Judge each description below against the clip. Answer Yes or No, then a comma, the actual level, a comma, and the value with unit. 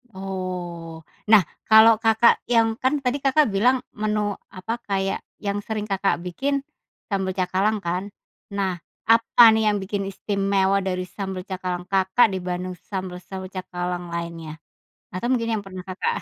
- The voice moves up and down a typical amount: Yes, average, 3.0 semitones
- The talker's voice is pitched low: No, high, 195 Hz